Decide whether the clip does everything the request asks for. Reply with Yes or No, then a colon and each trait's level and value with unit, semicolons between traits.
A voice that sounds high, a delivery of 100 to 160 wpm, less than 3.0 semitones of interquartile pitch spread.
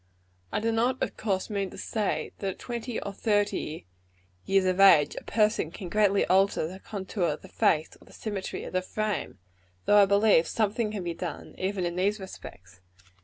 No: high, 195 Hz; average, 200 wpm; narrow, 2.6 semitones